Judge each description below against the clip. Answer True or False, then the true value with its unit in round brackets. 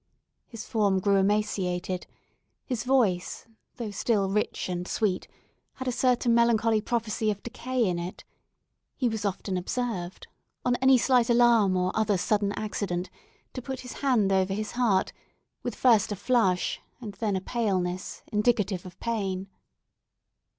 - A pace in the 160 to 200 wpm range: False (145 wpm)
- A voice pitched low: False (210 Hz)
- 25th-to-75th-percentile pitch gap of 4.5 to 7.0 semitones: False (3.9 semitones)